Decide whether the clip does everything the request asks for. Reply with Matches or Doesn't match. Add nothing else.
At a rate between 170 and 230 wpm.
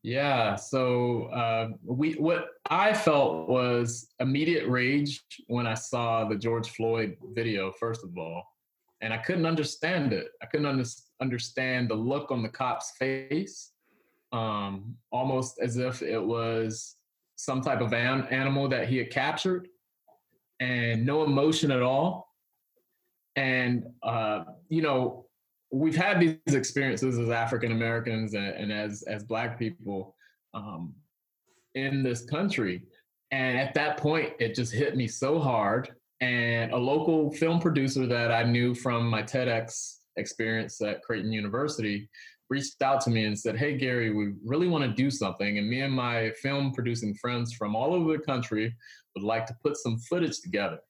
Doesn't match